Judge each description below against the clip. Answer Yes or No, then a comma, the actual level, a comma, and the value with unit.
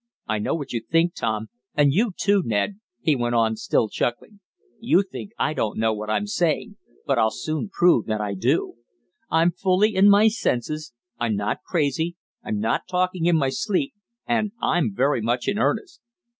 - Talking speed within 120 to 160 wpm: No, average, 185 wpm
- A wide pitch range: Yes, wide, 9.0 semitones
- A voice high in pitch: No, medium, 155 Hz